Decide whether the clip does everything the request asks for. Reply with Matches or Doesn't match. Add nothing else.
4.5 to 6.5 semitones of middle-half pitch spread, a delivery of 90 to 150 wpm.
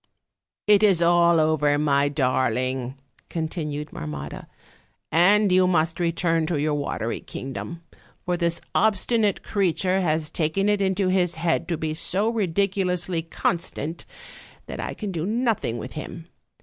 Doesn't match